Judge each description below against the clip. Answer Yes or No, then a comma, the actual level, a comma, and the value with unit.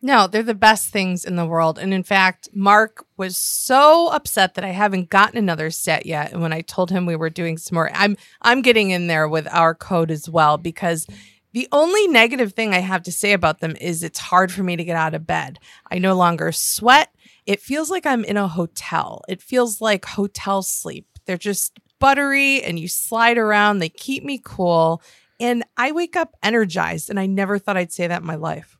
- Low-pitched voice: No, high, 190 Hz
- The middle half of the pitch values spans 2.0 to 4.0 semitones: No, average, 4.9 semitones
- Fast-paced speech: Yes, fast, 220 wpm